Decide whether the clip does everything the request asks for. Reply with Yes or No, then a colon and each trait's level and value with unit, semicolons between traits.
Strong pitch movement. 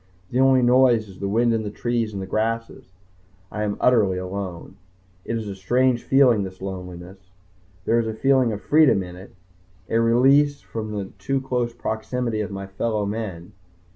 No: average, 3.9 semitones